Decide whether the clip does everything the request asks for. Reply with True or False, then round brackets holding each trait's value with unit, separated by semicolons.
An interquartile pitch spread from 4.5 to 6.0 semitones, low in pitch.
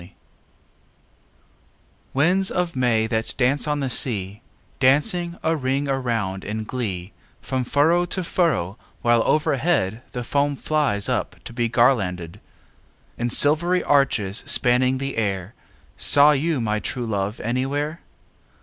True (5.0 semitones; 130 Hz)